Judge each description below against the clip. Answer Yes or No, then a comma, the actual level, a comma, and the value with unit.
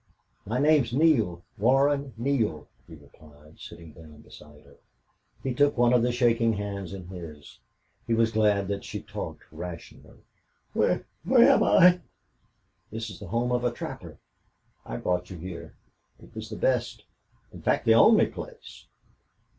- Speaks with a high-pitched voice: No, low, 110 Hz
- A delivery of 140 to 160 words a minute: Yes, average, 155 wpm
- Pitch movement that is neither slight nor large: No, wide, 6.2 semitones